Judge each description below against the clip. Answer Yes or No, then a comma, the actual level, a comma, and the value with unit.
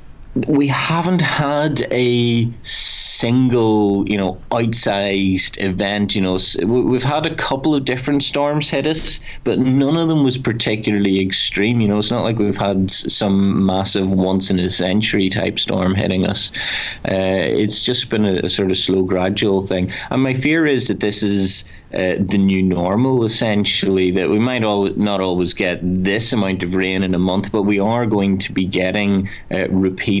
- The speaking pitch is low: Yes, low, 100 Hz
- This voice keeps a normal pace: Yes, average, 175 wpm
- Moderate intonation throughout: Yes, average, 4.2 semitones